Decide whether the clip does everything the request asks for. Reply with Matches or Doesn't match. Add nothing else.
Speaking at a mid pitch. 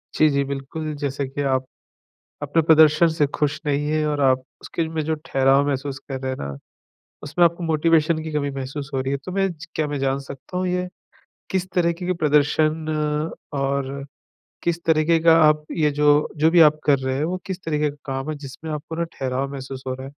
Matches